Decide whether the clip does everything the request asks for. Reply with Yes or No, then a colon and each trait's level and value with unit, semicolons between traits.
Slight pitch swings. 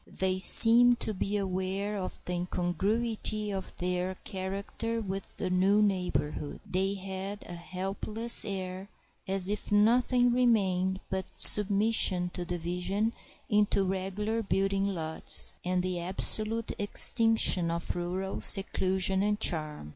Yes: narrow, 2.3 semitones